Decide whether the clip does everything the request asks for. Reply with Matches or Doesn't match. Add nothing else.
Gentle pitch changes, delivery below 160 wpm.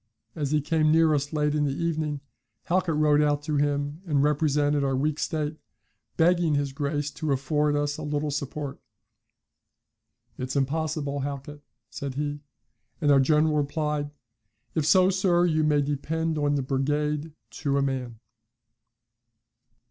Matches